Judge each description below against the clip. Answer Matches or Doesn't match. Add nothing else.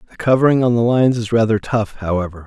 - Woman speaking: Doesn't match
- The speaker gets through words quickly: Matches